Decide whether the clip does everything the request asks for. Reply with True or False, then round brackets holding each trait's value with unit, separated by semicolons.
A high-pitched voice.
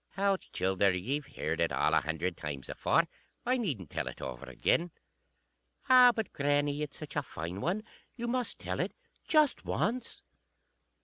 False (145 Hz)